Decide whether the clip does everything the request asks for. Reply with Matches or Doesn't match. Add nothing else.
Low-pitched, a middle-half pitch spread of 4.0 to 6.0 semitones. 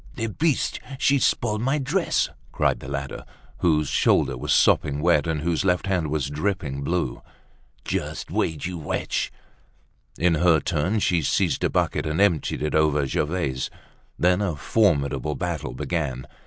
Matches